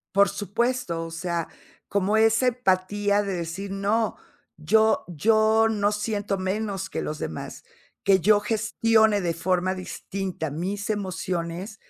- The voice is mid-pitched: No, high, 200 Hz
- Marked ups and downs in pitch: No, average, 3.0 semitones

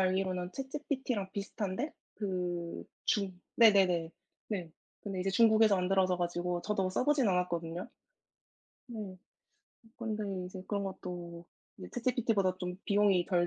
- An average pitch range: Yes, average, 3.0 semitones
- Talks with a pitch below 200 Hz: Yes, high, 190 Hz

